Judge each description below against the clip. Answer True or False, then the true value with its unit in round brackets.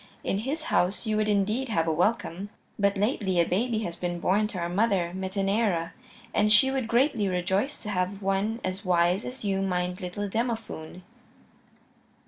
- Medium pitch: False (200 Hz)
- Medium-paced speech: True (170 wpm)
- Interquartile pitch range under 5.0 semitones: True (3.4 semitones)